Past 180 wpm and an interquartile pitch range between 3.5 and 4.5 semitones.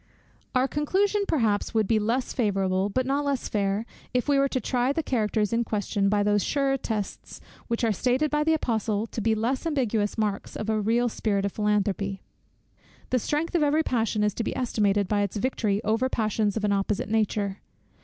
Yes: average, 195 wpm; average, 3.9 semitones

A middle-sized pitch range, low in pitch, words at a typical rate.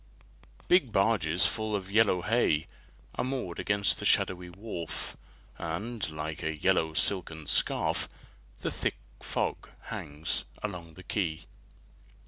No: average, 4.8 semitones; very low, 90 Hz; slow, 120 wpm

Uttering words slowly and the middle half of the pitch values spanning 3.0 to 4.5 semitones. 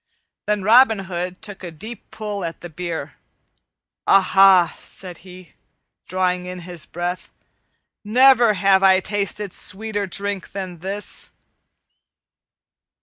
No: slow, 115 wpm; narrow, 2.4 semitones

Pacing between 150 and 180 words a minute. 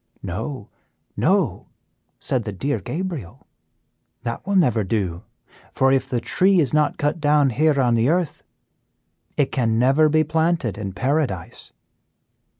No: average, 140 wpm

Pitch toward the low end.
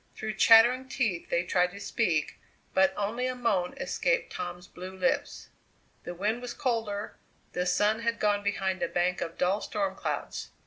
No: high, 205 Hz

